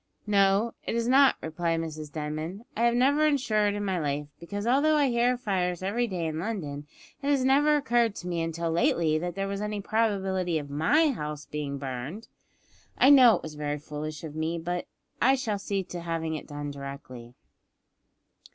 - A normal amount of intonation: No, wide, 7.0 semitones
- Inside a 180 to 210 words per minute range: Yes, average, 190 wpm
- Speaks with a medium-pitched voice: Yes, medium, 180 Hz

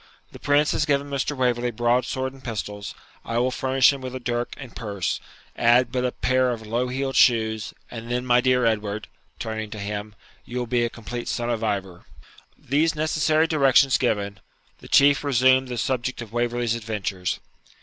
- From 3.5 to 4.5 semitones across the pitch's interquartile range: No, average, 2.8 semitones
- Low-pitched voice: Yes, low, 120 Hz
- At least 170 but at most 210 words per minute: Yes, average, 180 wpm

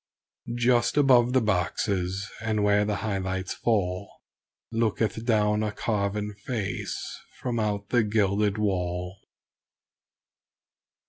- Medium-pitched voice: No, low, 105 Hz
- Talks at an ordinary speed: No, slow, 110 wpm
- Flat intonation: Yes, narrow, 2.3 semitones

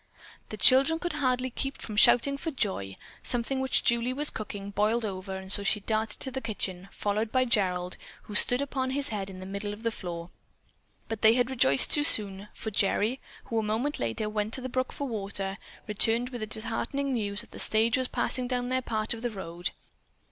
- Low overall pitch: No, high, 220 Hz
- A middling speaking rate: No, fast, 210 wpm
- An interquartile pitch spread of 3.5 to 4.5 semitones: Yes, average, 4.1 semitones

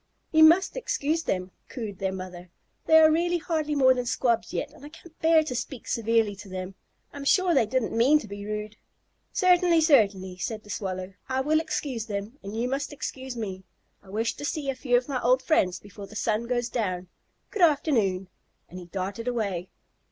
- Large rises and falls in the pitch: Yes, wide, 6.7 semitones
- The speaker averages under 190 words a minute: No, average, 200 wpm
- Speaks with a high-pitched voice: Yes, high, 235 Hz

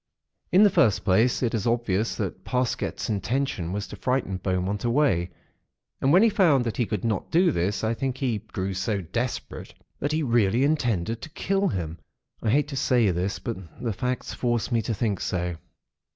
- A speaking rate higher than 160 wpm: Yes, average, 190 wpm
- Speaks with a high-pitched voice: No, low, 115 Hz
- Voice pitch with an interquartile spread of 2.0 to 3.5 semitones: No, average, 5.3 semitones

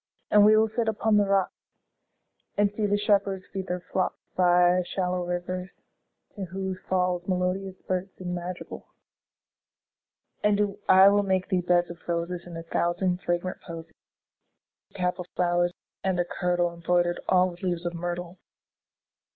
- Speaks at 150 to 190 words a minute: Yes, average, 160 wpm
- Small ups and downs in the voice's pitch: Yes, narrow, 1.6 semitones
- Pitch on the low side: No, medium, 180 Hz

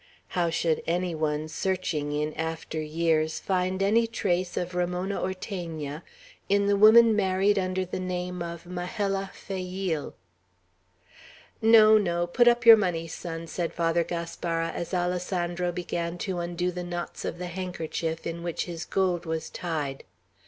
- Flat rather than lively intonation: Yes, narrow, 2.2 semitones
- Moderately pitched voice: Yes, medium, 175 Hz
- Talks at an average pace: Yes, average, 145 wpm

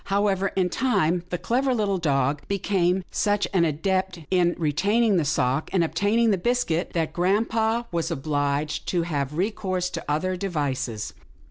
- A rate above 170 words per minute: No, average, 150 wpm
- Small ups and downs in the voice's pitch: No, average, 4.4 semitones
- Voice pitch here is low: No, medium, 180 Hz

